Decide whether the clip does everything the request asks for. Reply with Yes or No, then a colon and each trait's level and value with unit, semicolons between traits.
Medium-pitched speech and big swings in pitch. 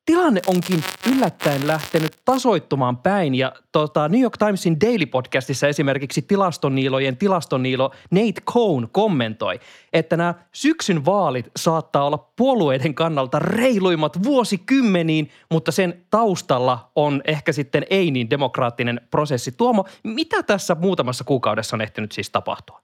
Yes: medium, 165 Hz; wide, 6.4 semitones